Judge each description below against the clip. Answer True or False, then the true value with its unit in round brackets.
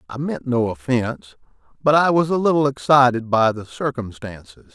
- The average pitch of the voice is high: False (125 Hz)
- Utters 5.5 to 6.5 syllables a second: False (5.1 syllables/s)